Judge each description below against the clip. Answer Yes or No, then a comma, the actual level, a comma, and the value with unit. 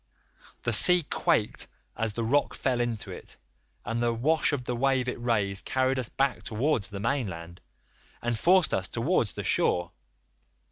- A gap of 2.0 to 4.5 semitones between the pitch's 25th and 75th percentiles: Yes, average, 3.6 semitones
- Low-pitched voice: Yes, low, 120 Hz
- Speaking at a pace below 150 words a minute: No, average, 170 wpm